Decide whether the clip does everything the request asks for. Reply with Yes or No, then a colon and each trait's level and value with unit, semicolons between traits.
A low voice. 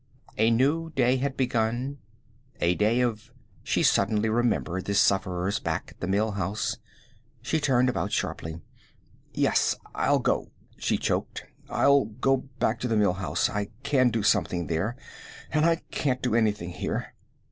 Yes: low, 110 Hz